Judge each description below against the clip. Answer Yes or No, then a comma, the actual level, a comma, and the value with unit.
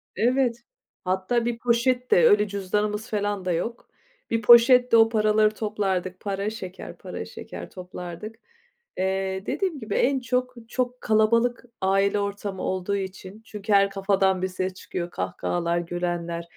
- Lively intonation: No, average, 3.6 semitones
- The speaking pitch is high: Yes, high, 205 Hz